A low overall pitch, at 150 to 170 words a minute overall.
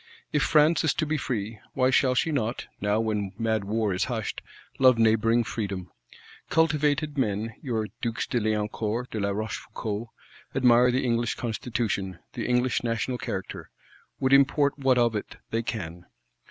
Yes: low, 115 Hz; average, 155 wpm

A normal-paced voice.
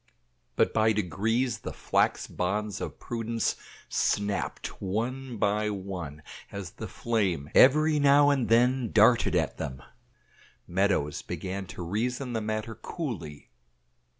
No: slow, 125 wpm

